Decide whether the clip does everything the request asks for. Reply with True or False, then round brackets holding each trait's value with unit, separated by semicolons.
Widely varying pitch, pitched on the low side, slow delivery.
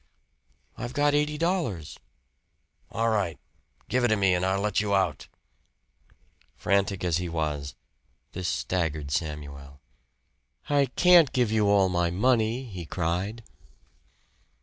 True (6.1 semitones; 95 Hz; 125 wpm)